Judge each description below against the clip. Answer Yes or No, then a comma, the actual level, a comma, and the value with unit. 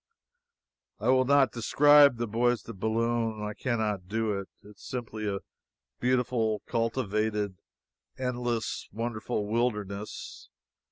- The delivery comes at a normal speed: No, slow, 120 wpm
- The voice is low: Yes, low, 115 Hz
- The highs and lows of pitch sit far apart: No, average, 2.7 semitones